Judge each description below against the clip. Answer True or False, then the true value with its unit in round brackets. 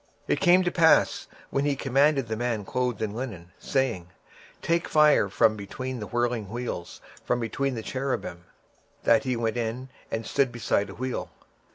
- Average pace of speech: True (185 wpm)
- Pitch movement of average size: True (3.5 semitones)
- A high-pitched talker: False (120 Hz)